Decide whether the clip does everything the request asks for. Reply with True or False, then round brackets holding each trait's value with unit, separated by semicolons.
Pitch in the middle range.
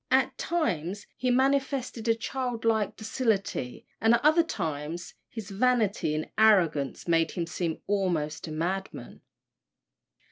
False (205 Hz)